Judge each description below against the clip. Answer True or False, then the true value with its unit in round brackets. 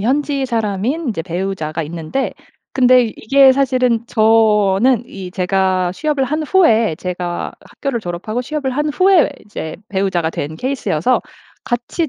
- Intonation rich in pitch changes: True (6.4 semitones)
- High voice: True (225 Hz)